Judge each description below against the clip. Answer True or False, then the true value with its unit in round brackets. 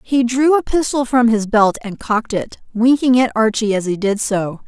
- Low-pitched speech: False (230 Hz)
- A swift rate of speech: True (220 wpm)